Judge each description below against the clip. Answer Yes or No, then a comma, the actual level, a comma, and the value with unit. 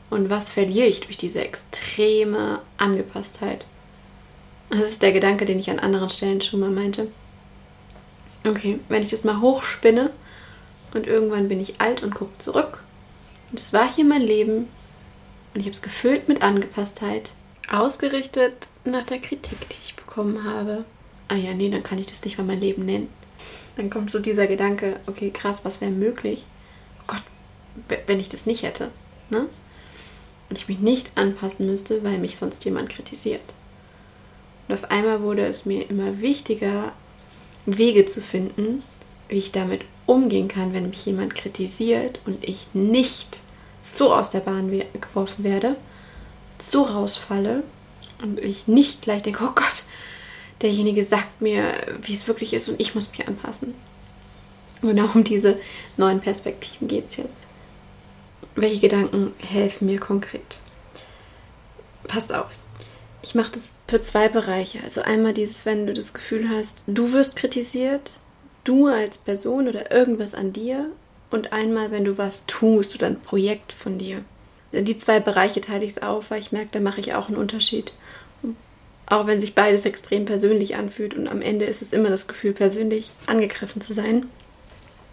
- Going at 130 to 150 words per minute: No, average, 165 wpm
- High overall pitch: Yes, high, 210 Hz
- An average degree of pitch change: No, narrow, 2.1 semitones